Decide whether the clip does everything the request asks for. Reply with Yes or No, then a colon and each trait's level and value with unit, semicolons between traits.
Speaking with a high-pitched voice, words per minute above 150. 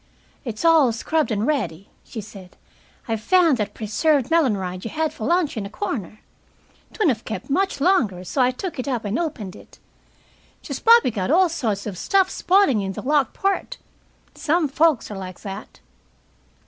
Yes: very high, 255 Hz; average, 175 wpm